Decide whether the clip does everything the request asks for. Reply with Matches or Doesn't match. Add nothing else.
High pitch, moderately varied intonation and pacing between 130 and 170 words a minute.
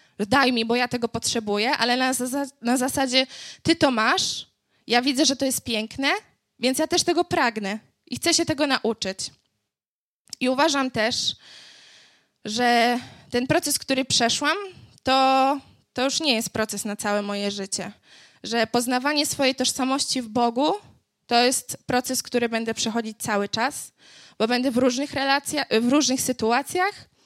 Matches